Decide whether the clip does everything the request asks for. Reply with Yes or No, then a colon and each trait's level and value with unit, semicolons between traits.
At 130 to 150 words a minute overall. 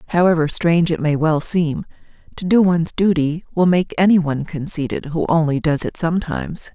No: average, 180 wpm